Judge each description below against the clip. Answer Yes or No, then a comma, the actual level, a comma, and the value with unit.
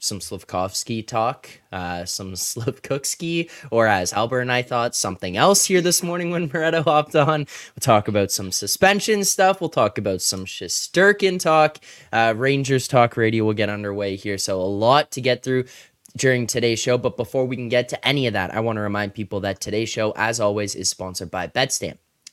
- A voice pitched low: Yes, low, 120 Hz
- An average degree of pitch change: No, wide, 5.9 semitones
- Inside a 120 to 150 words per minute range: No, average, 195 wpm